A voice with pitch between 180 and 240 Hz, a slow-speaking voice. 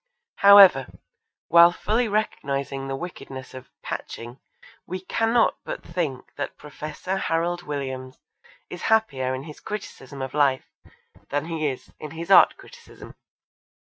No: medium, 150 Hz; slow, 130 wpm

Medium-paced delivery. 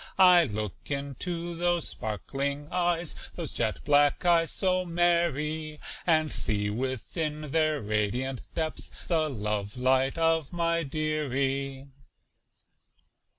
No: slow, 110 wpm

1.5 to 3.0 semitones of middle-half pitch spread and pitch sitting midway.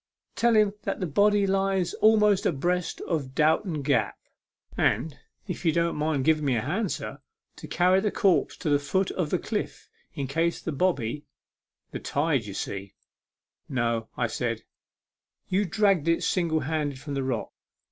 No: average, 5.1 semitones; medium, 160 Hz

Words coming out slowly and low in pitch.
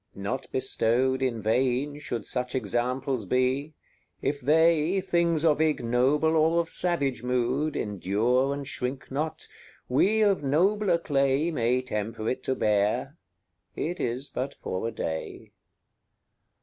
Yes: slow, 130 wpm; low, 130 Hz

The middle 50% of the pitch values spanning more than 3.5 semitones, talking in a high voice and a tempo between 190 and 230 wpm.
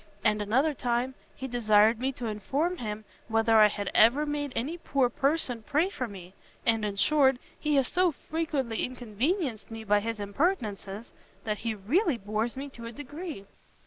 No: average, 5.2 semitones; high, 240 Hz; average, 175 wpm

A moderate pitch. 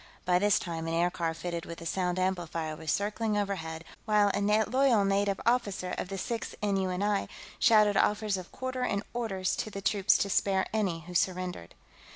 No: high, 195 Hz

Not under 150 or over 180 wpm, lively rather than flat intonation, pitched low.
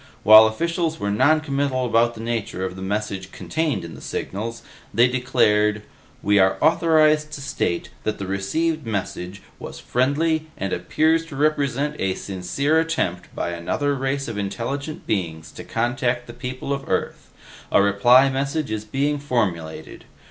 Yes: average, 155 wpm; wide, 6.0 semitones; low, 120 Hz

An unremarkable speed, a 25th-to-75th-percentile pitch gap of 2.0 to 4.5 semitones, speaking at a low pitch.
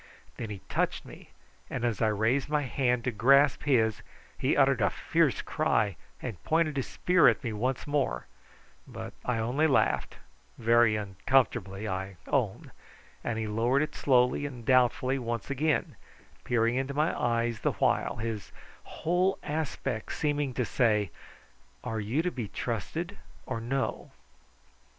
Yes: average, 150 wpm; average, 4.0 semitones; low, 120 Hz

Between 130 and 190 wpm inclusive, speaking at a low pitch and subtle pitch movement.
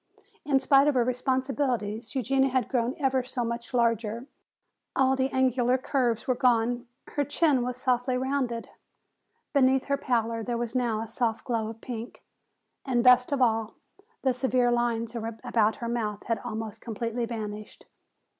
No: average, 155 wpm; high, 245 Hz; narrow, 2.2 semitones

